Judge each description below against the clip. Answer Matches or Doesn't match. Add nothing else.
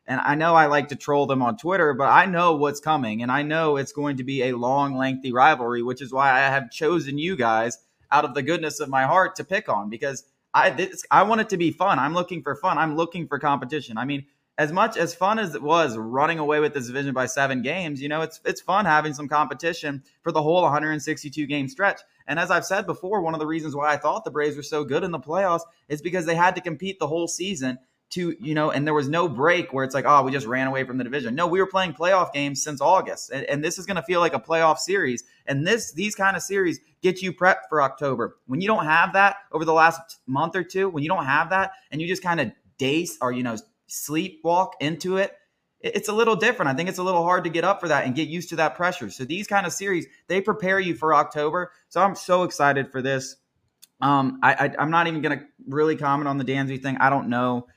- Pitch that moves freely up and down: Doesn't match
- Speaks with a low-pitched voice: Doesn't match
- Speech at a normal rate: Doesn't match